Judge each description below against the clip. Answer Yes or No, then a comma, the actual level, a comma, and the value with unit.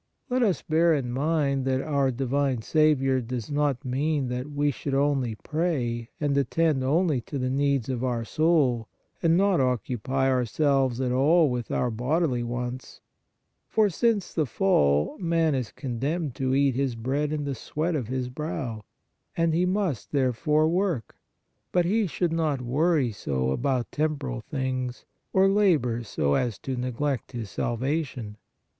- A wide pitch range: No, average, 4.0 semitones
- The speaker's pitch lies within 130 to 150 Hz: Yes, low, 135 Hz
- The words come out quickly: No, average, 165 wpm